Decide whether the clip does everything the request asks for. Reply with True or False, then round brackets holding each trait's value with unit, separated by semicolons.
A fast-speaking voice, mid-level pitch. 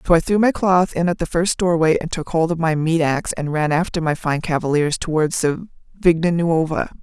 True (230 wpm; 165 Hz)